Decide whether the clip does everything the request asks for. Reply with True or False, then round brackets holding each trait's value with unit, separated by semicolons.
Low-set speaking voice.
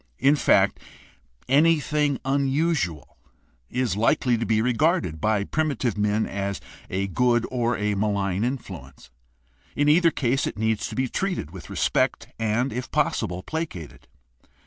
True (120 Hz)